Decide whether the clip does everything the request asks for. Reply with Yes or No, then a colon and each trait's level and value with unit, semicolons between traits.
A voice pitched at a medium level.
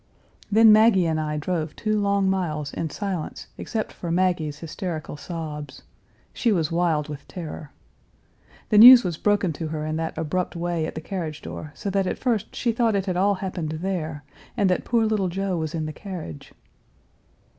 Yes: medium, 175 Hz